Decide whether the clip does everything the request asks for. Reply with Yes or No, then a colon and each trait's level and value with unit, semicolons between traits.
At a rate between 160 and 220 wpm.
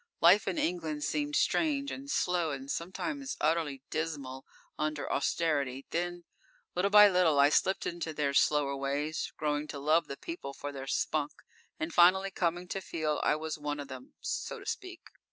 Yes: average, 170 wpm